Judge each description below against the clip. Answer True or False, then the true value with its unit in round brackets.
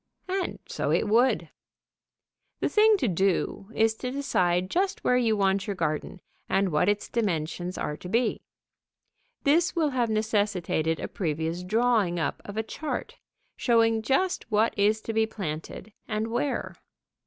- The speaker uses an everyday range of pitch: True (4.8 semitones)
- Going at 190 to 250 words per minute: False (155 wpm)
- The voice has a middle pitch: False (215 Hz)